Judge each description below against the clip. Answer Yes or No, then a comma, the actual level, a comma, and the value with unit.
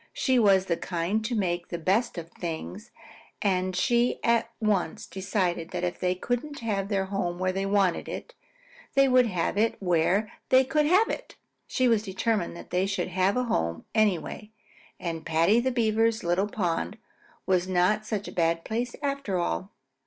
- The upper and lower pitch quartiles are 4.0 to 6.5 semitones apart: Yes, average, 4.4 semitones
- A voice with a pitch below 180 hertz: No, high, 195 Hz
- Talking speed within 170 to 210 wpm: Yes, average, 175 wpm